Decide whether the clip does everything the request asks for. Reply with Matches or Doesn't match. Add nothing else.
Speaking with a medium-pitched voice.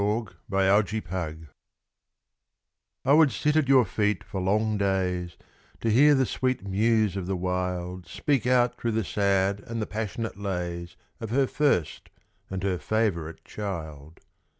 Doesn't match